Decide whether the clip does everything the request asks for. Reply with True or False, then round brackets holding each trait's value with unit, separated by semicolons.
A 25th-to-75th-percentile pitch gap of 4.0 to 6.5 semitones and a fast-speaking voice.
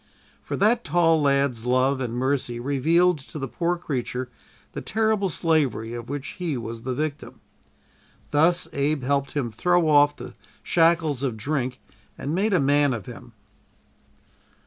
False (4.3 semitones; 150 wpm)